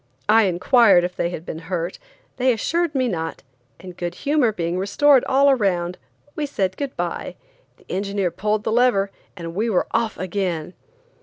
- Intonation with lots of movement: Yes, wide, 5.7 semitones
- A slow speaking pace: No, average, 170 wpm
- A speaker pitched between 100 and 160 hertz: No, high, 200 Hz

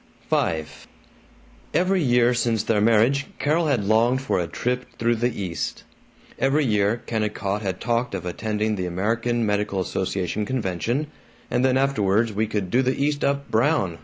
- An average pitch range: Yes, average, 4.1 semitones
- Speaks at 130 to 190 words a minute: Yes, average, 160 wpm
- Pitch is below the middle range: Yes, low, 115 Hz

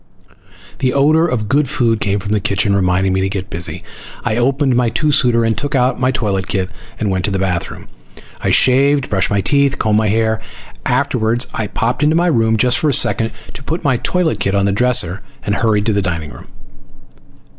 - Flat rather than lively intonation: No, average, 4.9 semitones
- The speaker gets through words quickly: Yes, fast, 215 wpm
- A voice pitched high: No, low, 110 Hz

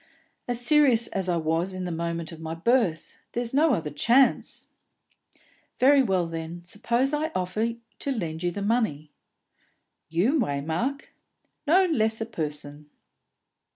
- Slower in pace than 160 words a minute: Yes, average, 140 wpm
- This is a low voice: No, high, 195 Hz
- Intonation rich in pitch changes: Yes, wide, 6.9 semitones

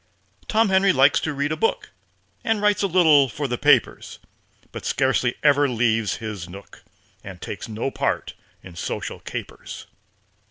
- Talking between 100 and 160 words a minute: Yes, average, 155 wpm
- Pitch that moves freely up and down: Yes, wide, 6.6 semitones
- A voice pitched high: No, low, 135 Hz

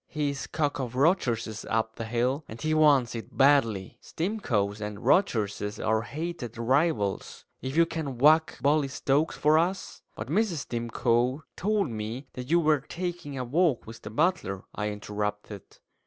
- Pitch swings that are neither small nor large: No, wide, 5.8 semitones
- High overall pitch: No, low, 130 Hz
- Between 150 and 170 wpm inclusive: Yes, average, 160 wpm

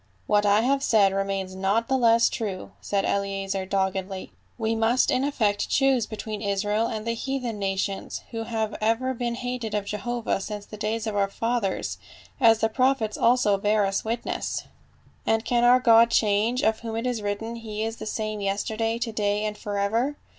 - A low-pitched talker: No, high, 220 Hz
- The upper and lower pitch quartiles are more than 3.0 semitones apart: No, narrow, 2.4 semitones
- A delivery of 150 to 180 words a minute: No, average, 190 wpm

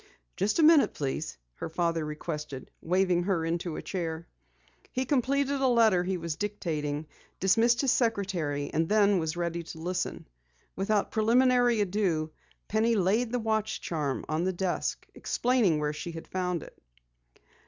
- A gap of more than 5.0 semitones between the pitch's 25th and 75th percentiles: Yes, wide, 5.5 semitones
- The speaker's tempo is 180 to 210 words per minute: No, average, 155 wpm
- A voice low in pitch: No, medium, 185 Hz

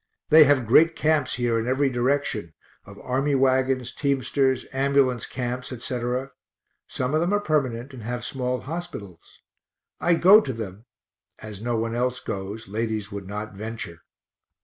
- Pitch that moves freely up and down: No, average, 3.5 semitones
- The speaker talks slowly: No, average, 150 wpm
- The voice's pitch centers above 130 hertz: No, low, 125 Hz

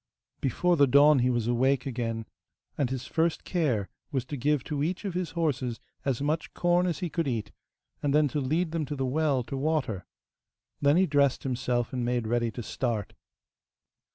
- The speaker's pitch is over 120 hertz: Yes, medium, 140 Hz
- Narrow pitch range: No, average, 4.3 semitones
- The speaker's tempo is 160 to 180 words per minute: No, average, 190 wpm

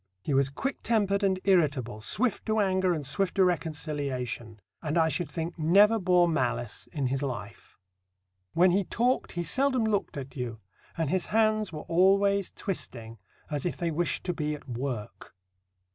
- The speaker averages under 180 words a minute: Yes, average, 170 wpm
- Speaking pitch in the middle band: Yes, medium, 170 Hz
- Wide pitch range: Yes, wide, 6.1 semitones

